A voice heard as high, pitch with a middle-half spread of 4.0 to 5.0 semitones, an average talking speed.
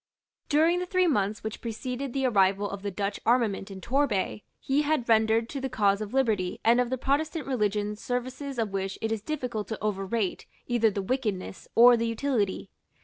Yes: high, 230 Hz; average, 4.3 semitones; average, 190 wpm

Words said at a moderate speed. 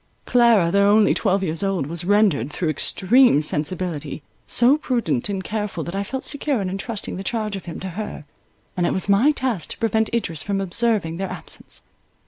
Yes: average, 190 wpm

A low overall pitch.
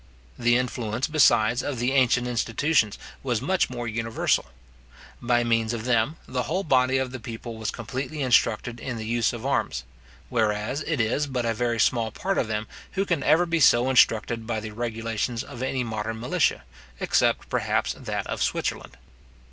Yes: low, 120 Hz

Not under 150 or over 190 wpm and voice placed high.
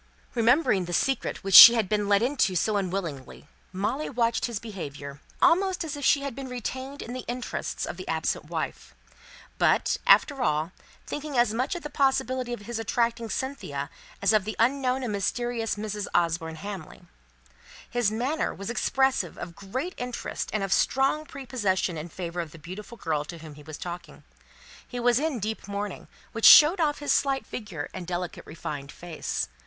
Yes: average, 180 wpm; high, 220 Hz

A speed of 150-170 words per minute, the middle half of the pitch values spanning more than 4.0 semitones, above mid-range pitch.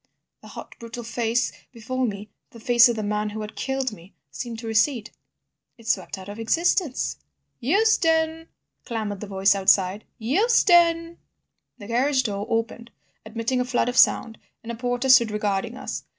No: average, 165 wpm; average, 3.5 semitones; high, 235 Hz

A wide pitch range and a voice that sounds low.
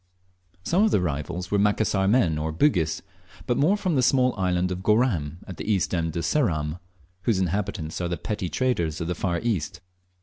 Yes: wide, 5.9 semitones; very low, 95 Hz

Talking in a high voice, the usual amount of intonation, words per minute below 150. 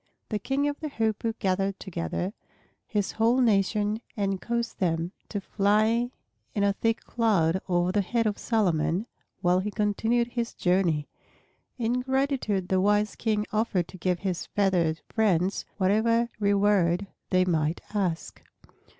Yes: high, 205 Hz; average, 3.5 semitones; average, 140 wpm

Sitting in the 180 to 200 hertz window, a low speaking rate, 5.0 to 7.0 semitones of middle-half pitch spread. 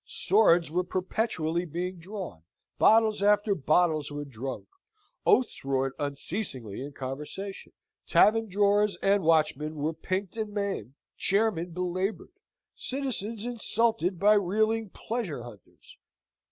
Yes: medium, 185 Hz; slow, 115 wpm; wide, 5.5 semitones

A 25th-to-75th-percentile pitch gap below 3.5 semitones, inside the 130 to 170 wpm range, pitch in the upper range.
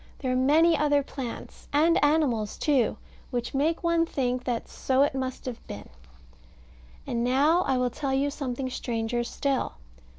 Yes: average, 2.9 semitones; average, 160 wpm; very high, 265 Hz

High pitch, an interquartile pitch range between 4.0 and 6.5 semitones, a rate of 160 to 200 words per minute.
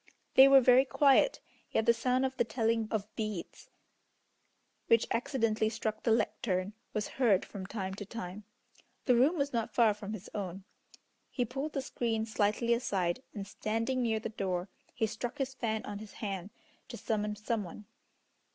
No: high, 220 Hz; average, 3.1 semitones; average, 170 wpm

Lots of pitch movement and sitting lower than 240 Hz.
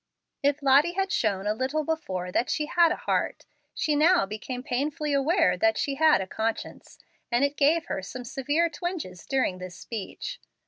No: wide, 6.1 semitones; very high, 280 Hz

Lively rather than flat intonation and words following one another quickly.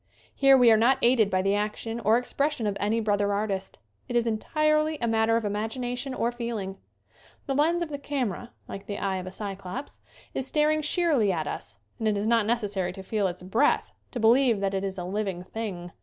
No: average, 4.2 semitones; fast, 215 wpm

